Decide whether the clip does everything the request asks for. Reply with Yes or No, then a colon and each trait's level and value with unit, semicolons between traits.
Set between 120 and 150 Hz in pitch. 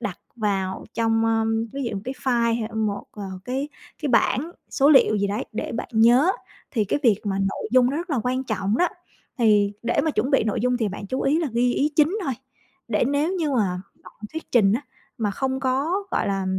No: high, 235 Hz